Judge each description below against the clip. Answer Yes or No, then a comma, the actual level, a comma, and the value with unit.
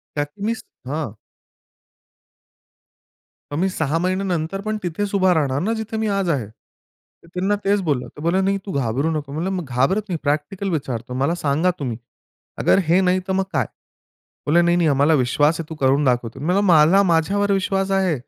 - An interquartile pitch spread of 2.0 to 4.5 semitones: No, average, 5.1 semitones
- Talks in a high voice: No, medium, 165 Hz